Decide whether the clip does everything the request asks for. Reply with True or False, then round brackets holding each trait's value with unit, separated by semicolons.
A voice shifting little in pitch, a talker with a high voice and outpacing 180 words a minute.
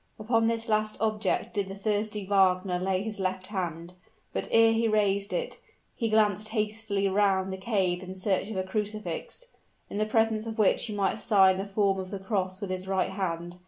True (2.3 semitones; 200 Hz; 195 wpm)